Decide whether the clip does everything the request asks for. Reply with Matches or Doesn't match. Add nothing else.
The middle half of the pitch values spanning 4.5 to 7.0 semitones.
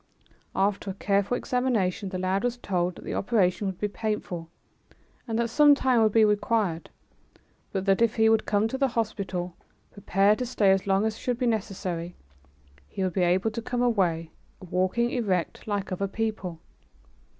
Doesn't match